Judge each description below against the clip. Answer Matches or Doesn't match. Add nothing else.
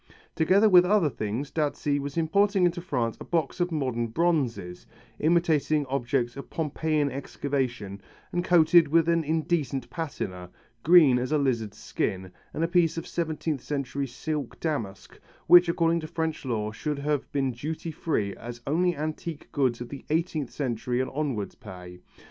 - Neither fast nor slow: Matches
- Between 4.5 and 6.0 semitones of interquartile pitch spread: Matches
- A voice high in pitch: Doesn't match